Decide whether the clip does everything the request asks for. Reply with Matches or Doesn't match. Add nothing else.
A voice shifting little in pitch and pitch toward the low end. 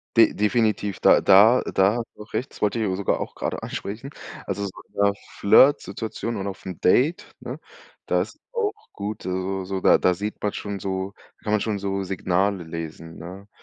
Matches